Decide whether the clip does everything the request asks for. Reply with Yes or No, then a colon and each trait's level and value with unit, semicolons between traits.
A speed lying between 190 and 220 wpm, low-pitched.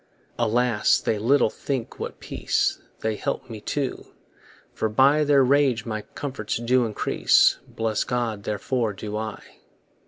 No: slow, 135 wpm; low, 115 Hz